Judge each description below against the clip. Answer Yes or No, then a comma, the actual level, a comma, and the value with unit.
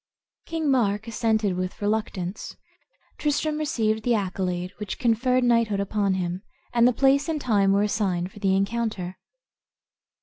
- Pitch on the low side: No, high, 215 Hz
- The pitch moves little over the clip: No, average, 3.9 semitones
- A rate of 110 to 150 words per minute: Yes, average, 140 wpm